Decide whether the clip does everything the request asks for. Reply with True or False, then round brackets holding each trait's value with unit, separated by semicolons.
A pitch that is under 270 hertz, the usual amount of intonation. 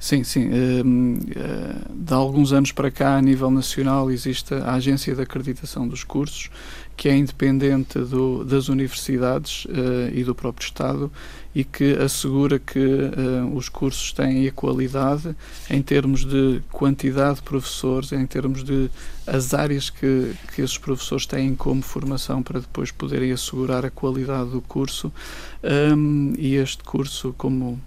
False (135 Hz; 1.1 semitones)